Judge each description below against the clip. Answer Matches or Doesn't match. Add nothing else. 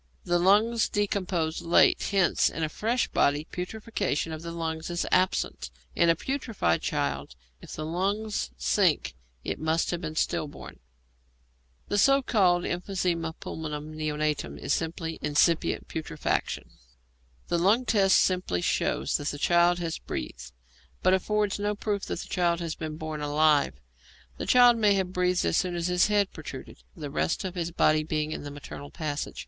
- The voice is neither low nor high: Matches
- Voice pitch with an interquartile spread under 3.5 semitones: Doesn't match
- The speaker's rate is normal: Matches